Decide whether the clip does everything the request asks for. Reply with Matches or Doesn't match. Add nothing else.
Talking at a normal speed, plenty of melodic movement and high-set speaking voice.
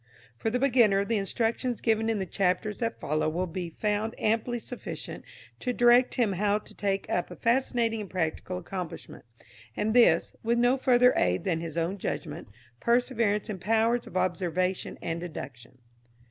Doesn't match